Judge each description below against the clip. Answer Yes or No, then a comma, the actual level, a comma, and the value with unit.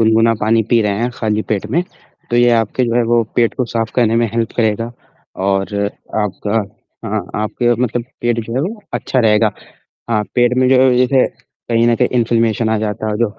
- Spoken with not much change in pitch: Yes, narrow, 1.8 semitones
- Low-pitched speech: Yes, low, 115 Hz